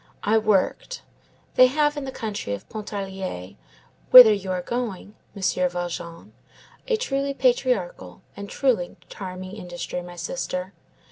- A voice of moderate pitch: No, high, 200 Hz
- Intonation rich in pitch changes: Yes, wide, 6.3 semitones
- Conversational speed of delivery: No, slow, 130 wpm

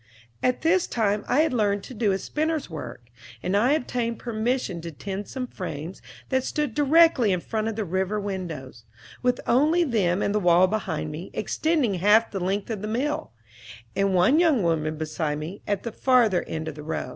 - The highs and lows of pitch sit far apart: Yes, wide, 5.9 semitones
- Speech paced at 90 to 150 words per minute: No, average, 195 wpm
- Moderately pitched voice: No, high, 205 Hz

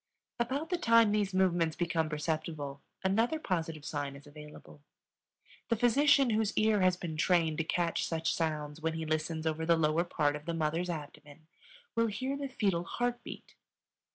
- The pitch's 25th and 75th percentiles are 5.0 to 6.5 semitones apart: Yes, wide, 5.5 semitones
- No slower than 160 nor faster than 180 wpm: Yes, average, 170 wpm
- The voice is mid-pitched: Yes, medium, 170 Hz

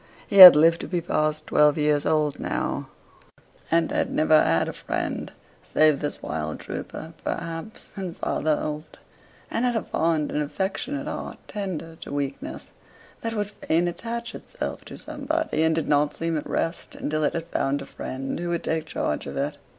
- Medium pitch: Yes, medium, 160 Hz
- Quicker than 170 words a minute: Yes, average, 180 wpm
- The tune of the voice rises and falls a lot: No, average, 4.1 semitones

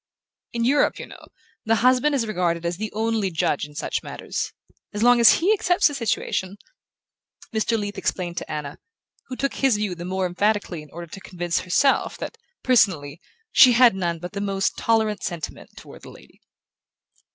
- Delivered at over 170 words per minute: Yes, average, 185 wpm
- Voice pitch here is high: Yes, high, 205 Hz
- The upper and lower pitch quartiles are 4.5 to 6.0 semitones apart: Yes, average, 5.1 semitones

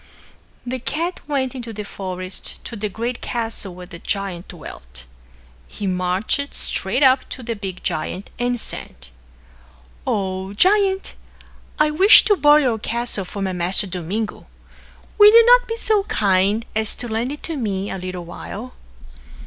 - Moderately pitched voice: No, high, 220 Hz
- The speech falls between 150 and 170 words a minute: Yes, average, 155 wpm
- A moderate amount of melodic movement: No, wide, 6.2 semitones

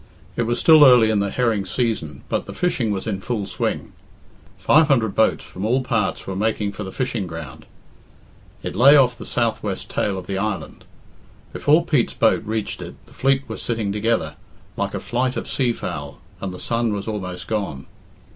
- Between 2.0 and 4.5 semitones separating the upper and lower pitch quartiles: Yes, average, 4.1 semitones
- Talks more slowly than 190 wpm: No, average, 195 wpm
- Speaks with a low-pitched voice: Yes, low, 110 Hz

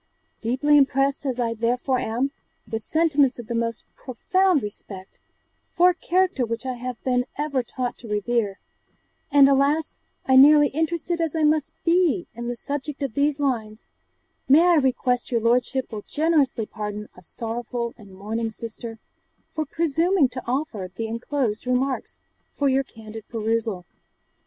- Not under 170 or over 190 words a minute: No, average, 155 wpm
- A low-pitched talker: No, very high, 255 Hz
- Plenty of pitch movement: No, average, 4.2 semitones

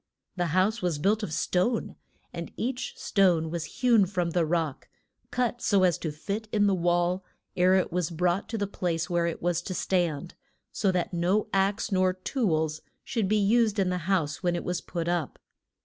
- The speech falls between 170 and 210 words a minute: Yes, average, 195 wpm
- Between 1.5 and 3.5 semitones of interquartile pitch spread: Yes, average, 2.9 semitones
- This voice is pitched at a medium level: Yes, medium, 180 Hz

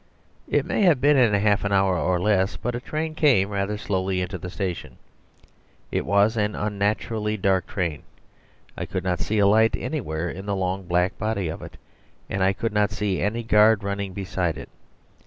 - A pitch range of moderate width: No, narrow, 2.3 semitones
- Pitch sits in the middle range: No, low, 100 Hz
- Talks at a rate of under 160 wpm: No, average, 195 wpm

